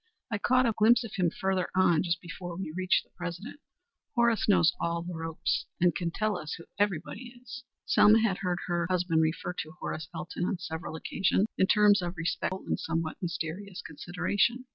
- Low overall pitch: No, medium, 180 Hz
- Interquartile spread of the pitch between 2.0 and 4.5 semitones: Yes, average, 3.3 semitones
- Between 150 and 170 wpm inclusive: No, average, 185 wpm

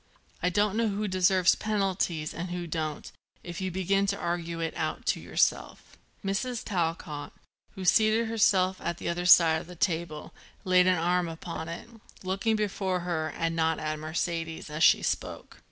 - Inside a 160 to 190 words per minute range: Yes, average, 175 wpm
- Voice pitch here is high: No, medium, 175 Hz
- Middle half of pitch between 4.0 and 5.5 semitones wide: No, average, 2.8 semitones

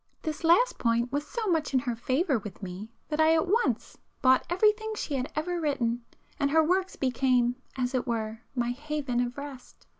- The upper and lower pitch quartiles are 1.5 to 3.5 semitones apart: No, average, 4.9 semitones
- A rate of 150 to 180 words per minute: No, average, 190 wpm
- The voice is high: Yes, very high, 275 Hz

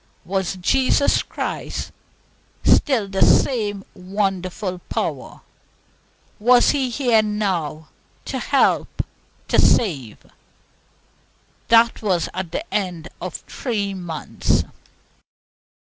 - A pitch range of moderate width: Yes, average, 4.0 semitones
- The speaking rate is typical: No, slow, 90 wpm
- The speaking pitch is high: Yes, high, 195 Hz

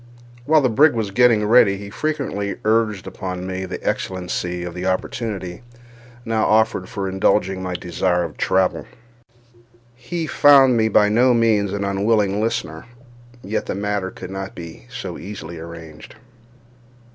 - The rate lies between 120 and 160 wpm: Yes, average, 145 wpm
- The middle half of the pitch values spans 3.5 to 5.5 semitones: Yes, average, 3.8 semitones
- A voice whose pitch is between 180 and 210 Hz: No, low, 100 Hz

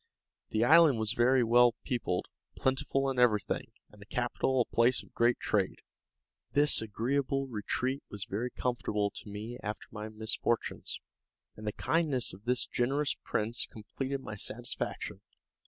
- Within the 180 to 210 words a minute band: No, average, 145 wpm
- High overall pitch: No, low, 120 Hz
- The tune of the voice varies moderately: Yes, average, 3.5 semitones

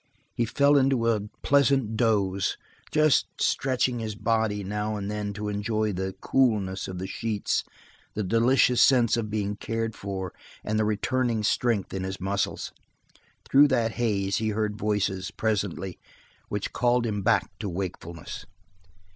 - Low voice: Yes, low, 105 Hz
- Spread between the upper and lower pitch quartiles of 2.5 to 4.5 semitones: Yes, average, 2.9 semitones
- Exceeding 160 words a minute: No, average, 145 wpm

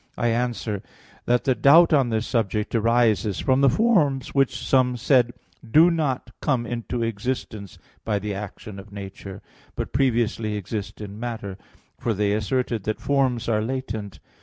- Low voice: Yes, low, 115 Hz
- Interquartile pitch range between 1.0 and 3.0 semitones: No, average, 3.7 semitones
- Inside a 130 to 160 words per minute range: Yes, average, 155 wpm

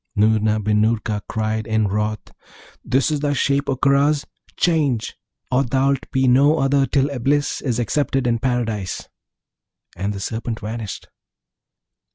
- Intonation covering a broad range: No, average, 4.2 semitones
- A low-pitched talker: Yes, low, 125 Hz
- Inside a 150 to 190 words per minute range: No, average, 140 wpm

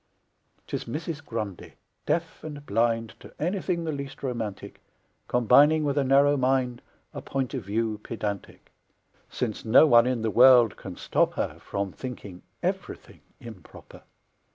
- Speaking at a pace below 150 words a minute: Yes, average, 140 wpm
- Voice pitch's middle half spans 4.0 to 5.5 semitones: Yes, average, 4.3 semitones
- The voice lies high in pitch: No, low, 125 Hz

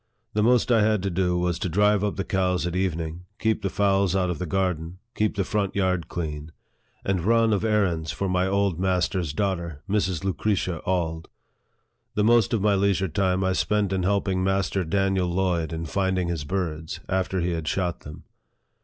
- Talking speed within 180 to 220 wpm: Yes, average, 190 wpm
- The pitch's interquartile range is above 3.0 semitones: No, narrow, 2.4 semitones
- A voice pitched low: Yes, very low, 95 Hz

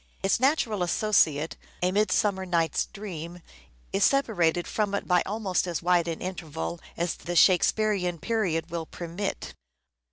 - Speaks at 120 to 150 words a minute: Yes, slow, 135 wpm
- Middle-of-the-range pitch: Yes, medium, 180 Hz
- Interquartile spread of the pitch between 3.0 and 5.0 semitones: Yes, average, 3.5 semitones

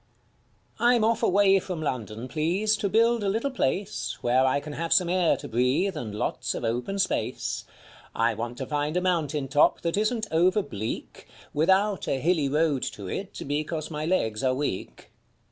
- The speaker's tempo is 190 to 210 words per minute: No, average, 180 wpm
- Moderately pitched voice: Yes, medium, 160 Hz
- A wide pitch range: Yes, wide, 6.8 semitones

